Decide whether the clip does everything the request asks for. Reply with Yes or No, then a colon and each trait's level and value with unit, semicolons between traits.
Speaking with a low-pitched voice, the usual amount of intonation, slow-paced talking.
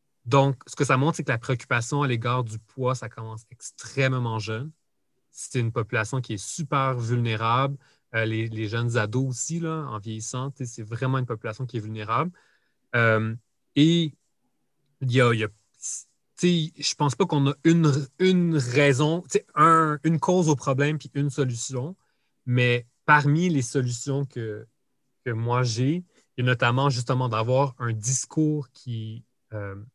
No: low, 130 Hz; average, 3.6 semitones; average, 160 wpm